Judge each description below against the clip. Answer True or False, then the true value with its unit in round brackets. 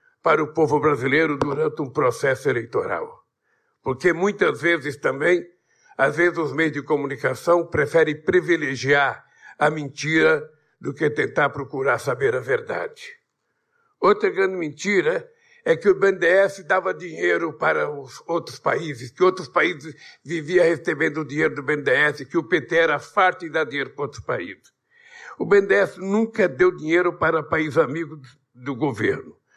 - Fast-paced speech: False (145 wpm)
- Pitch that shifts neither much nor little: False (6.4 semitones)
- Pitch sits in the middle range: True (170 Hz)